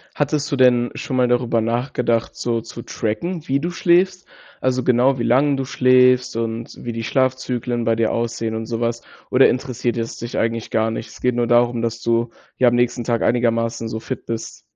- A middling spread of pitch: No, narrow, 1.8 semitones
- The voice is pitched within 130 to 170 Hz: No, low, 120 Hz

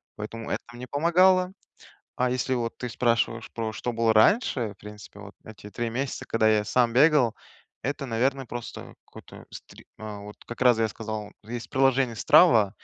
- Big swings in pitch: No, average, 3.0 semitones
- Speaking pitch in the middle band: No, low, 120 Hz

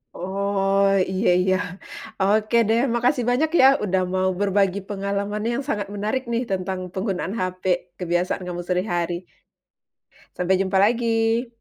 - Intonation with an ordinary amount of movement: Yes, average, 3.1 semitones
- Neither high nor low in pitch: No, high, 200 Hz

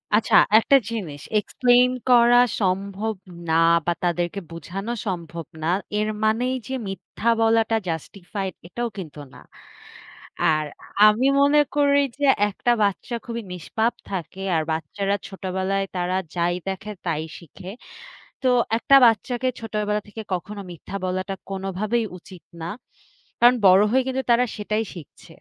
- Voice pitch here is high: Yes, high, 200 Hz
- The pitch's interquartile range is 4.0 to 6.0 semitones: Yes, average, 4.3 semitones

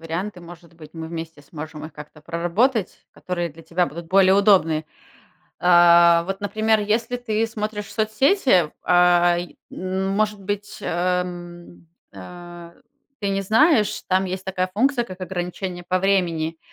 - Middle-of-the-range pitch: Yes, medium, 180 Hz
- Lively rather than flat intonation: No, average, 3.2 semitones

